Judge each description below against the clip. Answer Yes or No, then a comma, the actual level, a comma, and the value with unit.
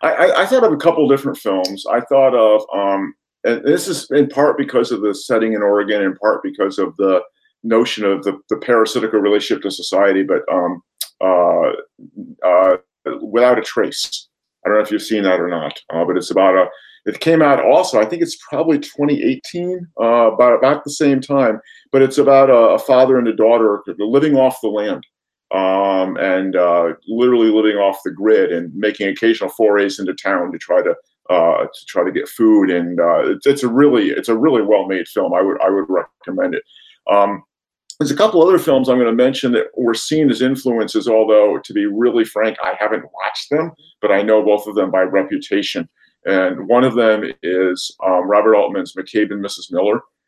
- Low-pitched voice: Yes, low, 115 Hz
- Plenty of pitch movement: Yes, wide, 6.3 semitones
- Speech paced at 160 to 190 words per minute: No, average, 200 wpm